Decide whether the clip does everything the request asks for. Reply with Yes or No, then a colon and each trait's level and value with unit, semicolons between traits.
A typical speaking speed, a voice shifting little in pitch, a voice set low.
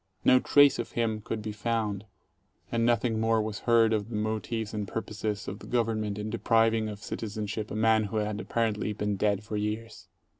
Yes: average, 190 wpm; narrow, 1.3 semitones; low, 110 Hz